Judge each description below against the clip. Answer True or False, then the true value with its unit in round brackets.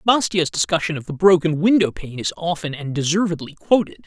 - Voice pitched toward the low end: False (170 Hz)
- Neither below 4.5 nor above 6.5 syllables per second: True (5.6 syllables/s)